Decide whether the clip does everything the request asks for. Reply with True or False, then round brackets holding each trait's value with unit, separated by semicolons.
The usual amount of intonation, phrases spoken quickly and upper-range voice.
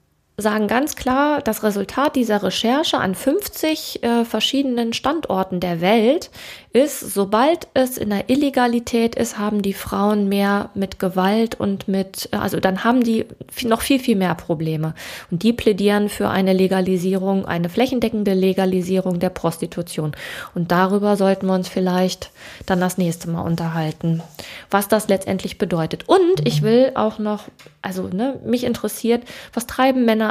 False (4.2 semitones; 150 wpm; 205 Hz)